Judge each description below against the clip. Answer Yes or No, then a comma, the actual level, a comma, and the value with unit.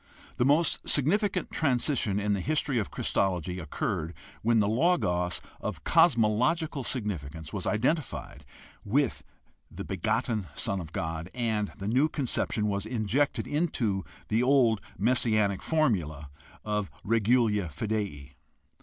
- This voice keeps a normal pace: No, slow, 125 wpm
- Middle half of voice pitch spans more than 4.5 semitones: Yes, average, 5.3 semitones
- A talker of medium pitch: No, low, 110 Hz